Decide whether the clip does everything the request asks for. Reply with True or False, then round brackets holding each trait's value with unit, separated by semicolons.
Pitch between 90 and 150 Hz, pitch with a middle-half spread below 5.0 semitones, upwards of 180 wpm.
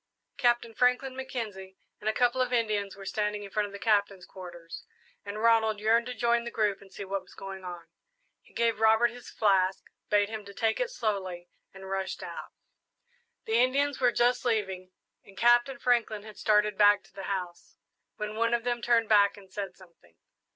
False (210 Hz; 3.3 semitones; 190 wpm)